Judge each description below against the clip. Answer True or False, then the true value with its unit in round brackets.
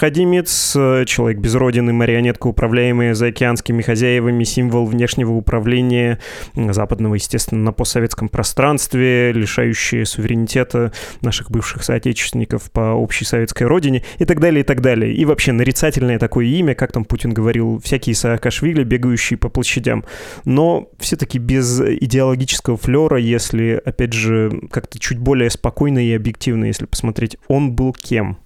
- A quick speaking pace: False (135 wpm)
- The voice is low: True (120 Hz)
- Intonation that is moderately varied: False (2.0 semitones)